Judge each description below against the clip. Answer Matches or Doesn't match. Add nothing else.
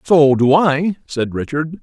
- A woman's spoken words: Doesn't match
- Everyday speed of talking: Matches